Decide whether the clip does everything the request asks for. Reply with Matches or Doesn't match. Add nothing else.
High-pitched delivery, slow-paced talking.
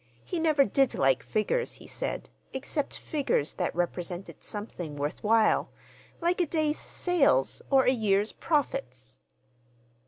Matches